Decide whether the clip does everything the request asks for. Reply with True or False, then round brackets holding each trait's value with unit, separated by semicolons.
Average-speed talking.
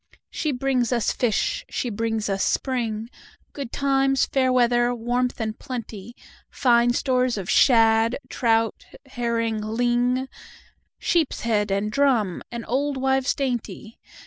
False (105 wpm)